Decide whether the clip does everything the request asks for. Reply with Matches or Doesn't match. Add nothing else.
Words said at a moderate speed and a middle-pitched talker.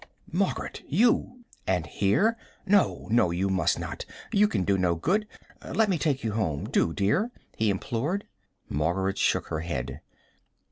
Doesn't match